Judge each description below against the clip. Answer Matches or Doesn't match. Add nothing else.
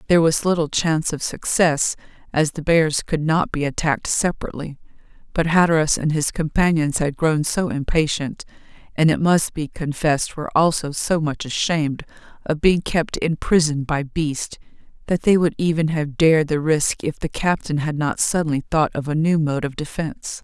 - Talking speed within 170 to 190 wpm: Matches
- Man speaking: Doesn't match